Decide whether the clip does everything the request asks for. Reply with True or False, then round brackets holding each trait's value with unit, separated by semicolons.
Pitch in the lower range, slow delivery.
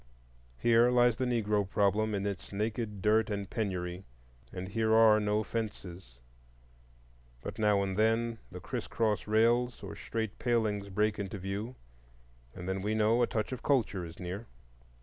False (105 Hz; 155 wpm)